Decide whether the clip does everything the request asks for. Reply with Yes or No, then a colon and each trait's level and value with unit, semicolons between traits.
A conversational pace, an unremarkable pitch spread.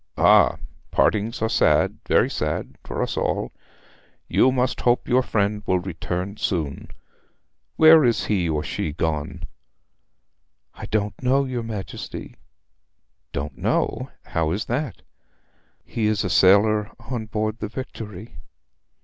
No: slow, 130 wpm; average, 4.7 semitones